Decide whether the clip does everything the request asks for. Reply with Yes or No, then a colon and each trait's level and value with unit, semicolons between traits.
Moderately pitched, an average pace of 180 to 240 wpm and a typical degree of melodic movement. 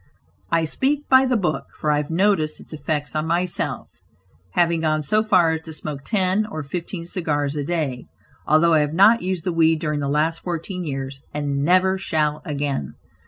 Yes: medium, 160 Hz; average, 190 wpm; average, 3.5 semitones